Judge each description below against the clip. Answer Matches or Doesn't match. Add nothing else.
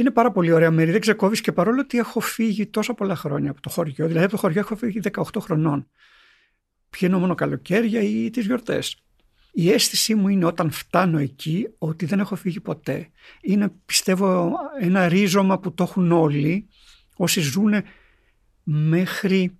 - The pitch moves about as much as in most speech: Matches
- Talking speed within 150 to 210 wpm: Matches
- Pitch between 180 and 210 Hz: Matches